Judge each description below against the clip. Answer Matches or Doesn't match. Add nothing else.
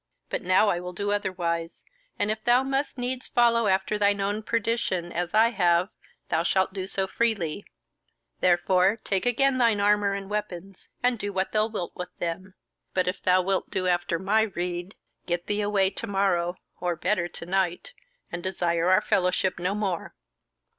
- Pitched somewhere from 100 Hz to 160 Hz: Doesn't match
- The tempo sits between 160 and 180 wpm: Matches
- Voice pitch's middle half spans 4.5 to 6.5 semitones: Doesn't match